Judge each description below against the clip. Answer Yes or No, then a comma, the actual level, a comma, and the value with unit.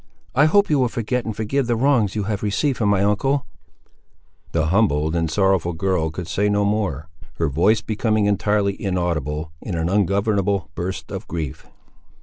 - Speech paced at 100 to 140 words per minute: No, average, 170 wpm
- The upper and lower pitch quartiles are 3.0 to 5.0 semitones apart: Yes, average, 4.2 semitones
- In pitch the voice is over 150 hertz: No, low, 100 Hz